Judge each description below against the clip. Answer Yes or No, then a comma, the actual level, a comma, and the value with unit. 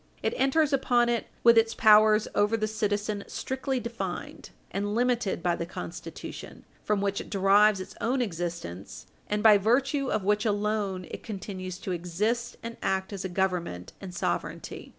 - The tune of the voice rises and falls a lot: No, average, 3.4 semitones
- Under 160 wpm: No, average, 165 wpm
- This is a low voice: No, high, 210 Hz